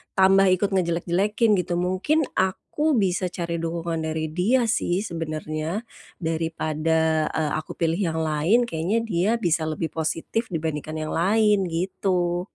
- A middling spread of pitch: Yes, average, 3.2 semitones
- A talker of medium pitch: Yes, medium, 175 Hz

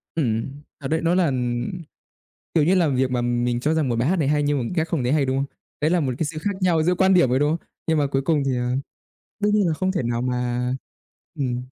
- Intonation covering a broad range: No, average, 4.6 semitones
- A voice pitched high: No, medium, 145 Hz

